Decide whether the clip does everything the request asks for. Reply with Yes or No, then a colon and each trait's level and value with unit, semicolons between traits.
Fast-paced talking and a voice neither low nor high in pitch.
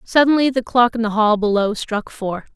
No: fast, 210 wpm; high, 230 Hz